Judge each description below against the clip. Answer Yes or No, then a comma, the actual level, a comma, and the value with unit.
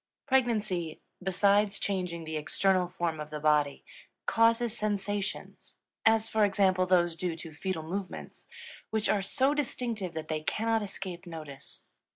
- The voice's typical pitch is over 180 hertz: Yes, high, 190 Hz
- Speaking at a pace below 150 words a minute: Yes, average, 140 wpm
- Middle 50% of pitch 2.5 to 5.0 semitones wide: Yes, average, 4.4 semitones